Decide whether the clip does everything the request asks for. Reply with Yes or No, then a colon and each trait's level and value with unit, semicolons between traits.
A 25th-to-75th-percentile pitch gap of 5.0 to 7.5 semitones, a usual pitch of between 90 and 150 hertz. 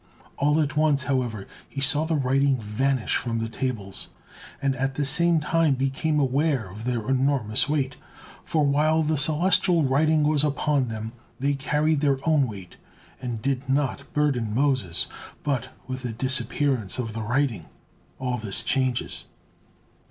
No: average, 3.2 semitones; low, 135 Hz